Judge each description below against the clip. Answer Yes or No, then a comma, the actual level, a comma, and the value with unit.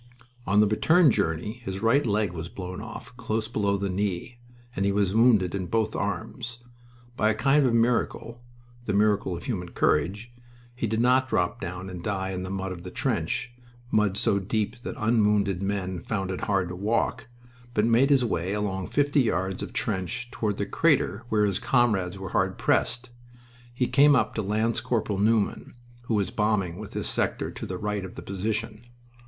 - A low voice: Yes, low, 105 Hz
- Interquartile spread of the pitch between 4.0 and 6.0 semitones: No, average, 3.4 semitones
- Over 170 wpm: Yes, average, 190 wpm